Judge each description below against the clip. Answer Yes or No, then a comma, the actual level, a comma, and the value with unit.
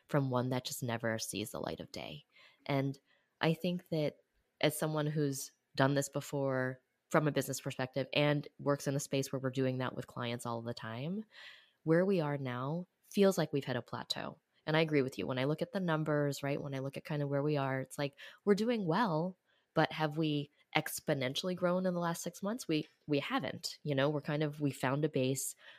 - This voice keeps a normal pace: No, fast, 225 wpm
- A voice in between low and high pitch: Yes, medium, 145 Hz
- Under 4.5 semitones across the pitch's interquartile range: Yes, average, 3.0 semitones